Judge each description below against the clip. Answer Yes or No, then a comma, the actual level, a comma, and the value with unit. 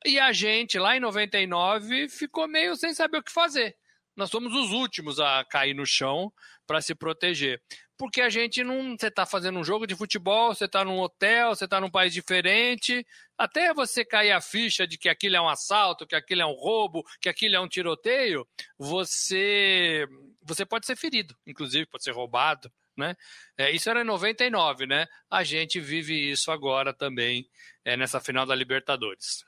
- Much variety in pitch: Yes, wide, 6.7 semitones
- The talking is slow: No, fast, 185 wpm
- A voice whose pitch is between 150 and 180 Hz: No, high, 190 Hz